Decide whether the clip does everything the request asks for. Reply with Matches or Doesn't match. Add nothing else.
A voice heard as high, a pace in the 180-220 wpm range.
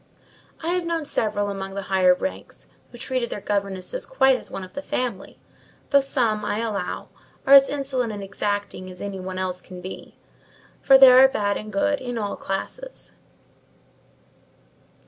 Doesn't match